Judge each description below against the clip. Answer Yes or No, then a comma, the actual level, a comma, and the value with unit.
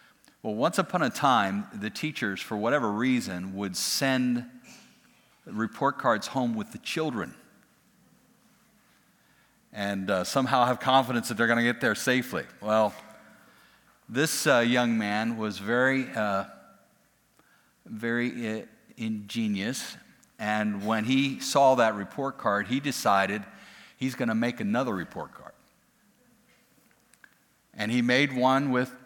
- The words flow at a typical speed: No, slow, 130 wpm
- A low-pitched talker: Yes, low, 120 Hz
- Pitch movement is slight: No, average, 3.3 semitones